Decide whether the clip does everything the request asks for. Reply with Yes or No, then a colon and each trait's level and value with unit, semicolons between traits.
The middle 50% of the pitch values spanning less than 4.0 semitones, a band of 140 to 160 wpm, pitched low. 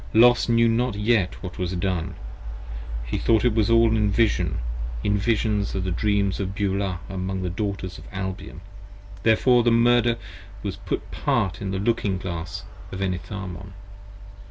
Yes: average, 3.3 semitones; average, 155 wpm; low, 100 Hz